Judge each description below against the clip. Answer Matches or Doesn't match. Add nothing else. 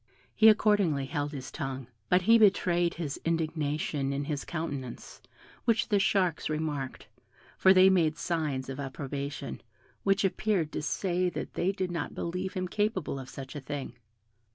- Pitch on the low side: Doesn't match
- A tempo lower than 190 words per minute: Matches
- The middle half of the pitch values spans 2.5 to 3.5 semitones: Doesn't match